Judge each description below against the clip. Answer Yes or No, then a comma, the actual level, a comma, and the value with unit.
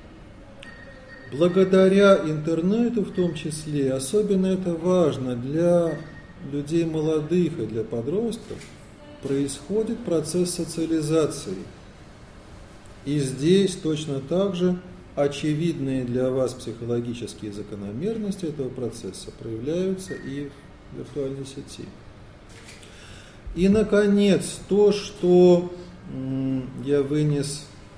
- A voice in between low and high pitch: Yes, medium, 150 Hz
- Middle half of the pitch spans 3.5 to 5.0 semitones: No, wide, 5.6 semitones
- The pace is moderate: No, slow, 85 wpm